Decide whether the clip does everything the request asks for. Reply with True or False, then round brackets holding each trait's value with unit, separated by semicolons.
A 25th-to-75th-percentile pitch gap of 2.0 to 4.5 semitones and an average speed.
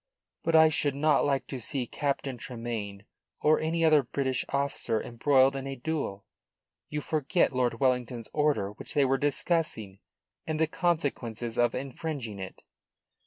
True (4.1 semitones; 150 wpm)